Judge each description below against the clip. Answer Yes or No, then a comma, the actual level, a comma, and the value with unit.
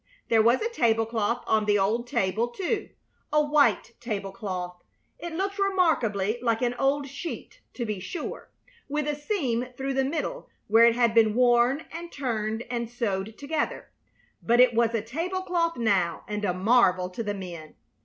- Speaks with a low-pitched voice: No, high, 235 Hz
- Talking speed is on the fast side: No, average, 165 wpm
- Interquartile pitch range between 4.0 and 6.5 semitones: Yes, average, 5.3 semitones